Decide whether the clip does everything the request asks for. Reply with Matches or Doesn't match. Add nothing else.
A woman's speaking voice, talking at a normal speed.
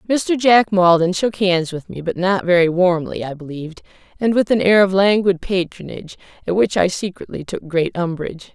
Matches